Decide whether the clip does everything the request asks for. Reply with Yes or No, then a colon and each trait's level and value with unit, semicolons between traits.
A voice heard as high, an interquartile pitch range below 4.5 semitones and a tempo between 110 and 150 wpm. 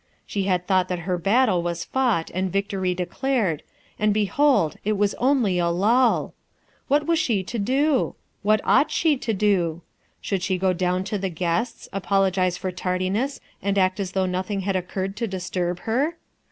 No: high, 195 Hz; average, 3.5 semitones; average, 175 wpm